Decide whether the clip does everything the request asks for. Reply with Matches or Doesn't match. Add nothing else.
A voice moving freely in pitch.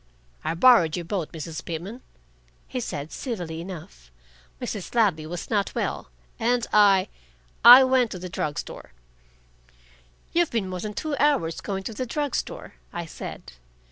Matches